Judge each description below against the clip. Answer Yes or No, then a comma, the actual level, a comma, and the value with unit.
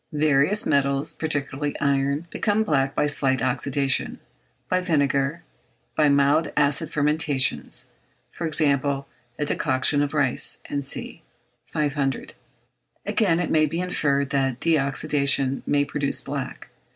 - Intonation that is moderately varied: No, narrow, 2.0 semitones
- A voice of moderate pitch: Yes, medium, 145 Hz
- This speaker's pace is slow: Yes, slow, 125 wpm